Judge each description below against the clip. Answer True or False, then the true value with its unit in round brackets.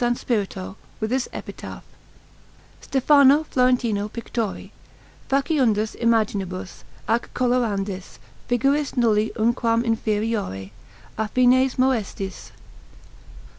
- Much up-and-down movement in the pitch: False (3.3 semitones)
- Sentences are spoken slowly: True (75 wpm)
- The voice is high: True (230 Hz)